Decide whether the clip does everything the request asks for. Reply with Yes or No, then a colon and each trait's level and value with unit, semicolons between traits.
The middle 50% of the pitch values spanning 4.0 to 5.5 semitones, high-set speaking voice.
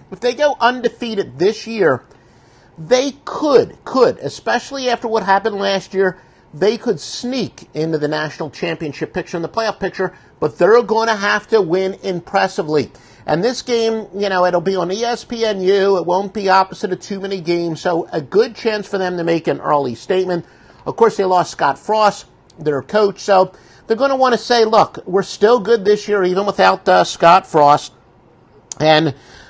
Yes: average, 5.0 semitones; high, 195 Hz